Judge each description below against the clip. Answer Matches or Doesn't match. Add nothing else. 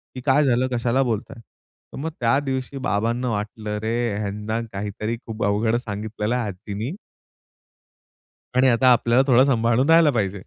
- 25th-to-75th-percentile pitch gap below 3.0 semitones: Doesn't match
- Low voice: Matches